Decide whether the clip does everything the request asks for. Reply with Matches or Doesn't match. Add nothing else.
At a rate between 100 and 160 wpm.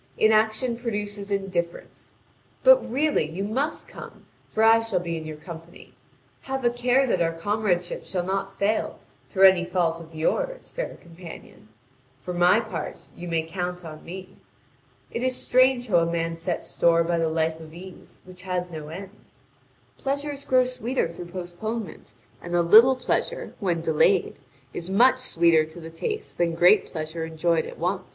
Doesn't match